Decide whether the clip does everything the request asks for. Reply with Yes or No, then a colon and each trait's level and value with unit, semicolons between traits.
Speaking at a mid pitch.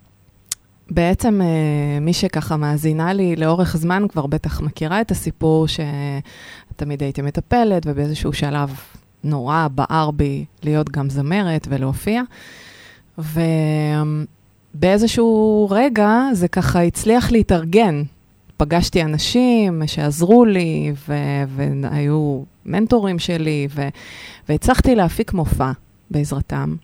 Yes: medium, 155 Hz